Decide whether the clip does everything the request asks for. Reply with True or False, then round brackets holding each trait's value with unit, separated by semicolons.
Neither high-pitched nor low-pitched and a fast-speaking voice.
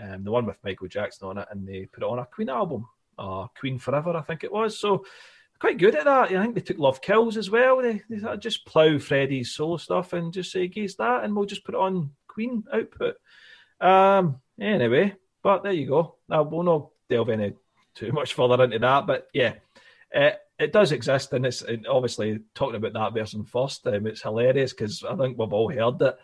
True (155 Hz; 225 wpm)